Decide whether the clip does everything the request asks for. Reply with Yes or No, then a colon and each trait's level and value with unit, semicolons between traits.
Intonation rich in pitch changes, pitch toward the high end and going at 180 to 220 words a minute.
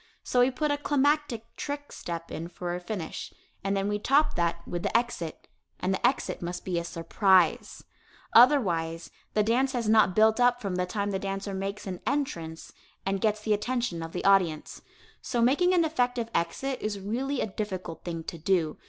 Yes: wide, 5.8 semitones; high, 205 Hz; average, 190 wpm